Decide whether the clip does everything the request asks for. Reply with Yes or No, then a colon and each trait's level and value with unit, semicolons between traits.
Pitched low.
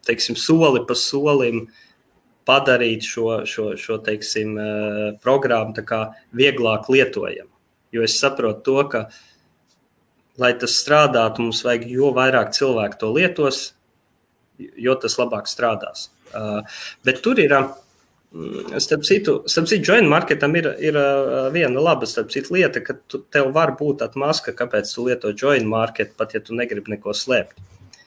Yes: low, 125 Hz